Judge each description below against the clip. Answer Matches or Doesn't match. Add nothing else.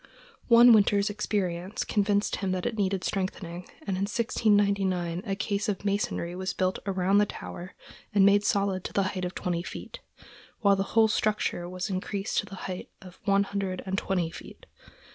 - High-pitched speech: Matches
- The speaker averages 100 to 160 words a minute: Doesn't match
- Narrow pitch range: Matches